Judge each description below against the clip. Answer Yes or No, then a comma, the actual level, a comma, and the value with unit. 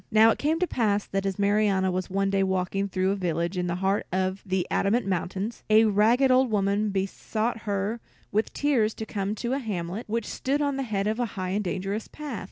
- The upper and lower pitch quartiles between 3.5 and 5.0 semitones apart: No, average, 2.9 semitones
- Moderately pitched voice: No, high, 205 Hz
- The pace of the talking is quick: Yes, fast, 220 wpm